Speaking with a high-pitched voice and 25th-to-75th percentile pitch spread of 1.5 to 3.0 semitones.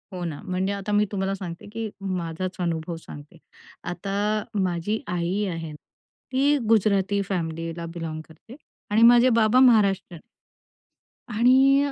No: high, 195 Hz; average, 4.2 semitones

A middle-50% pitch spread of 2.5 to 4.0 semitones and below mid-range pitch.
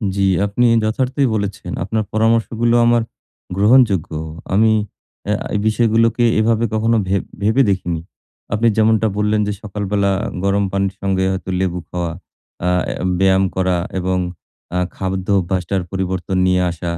Yes: average, 2.9 semitones; low, 100 Hz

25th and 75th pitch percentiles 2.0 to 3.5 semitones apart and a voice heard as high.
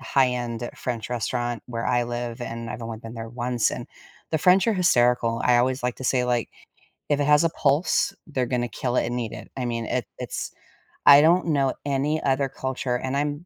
No: average, 2.8 semitones; low, 125 Hz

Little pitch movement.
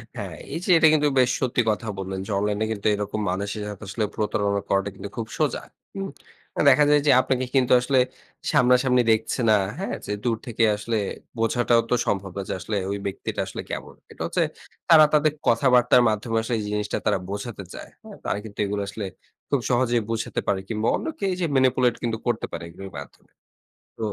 No: average, 3.7 semitones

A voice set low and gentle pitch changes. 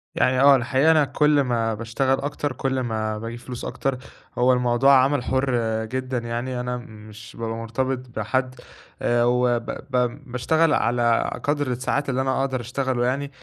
Yes: low, 125 Hz; narrow, 2.2 semitones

